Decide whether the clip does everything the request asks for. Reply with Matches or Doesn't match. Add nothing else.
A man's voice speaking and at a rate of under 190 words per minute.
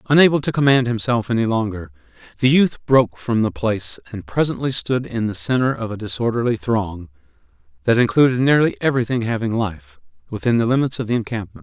Matches